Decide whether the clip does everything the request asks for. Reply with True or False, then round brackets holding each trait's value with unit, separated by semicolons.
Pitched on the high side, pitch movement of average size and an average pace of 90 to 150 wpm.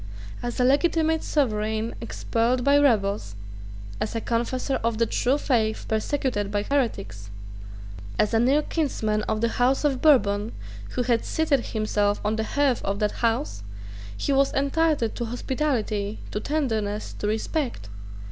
True (235 Hz; 4.5 semitones; 145 wpm)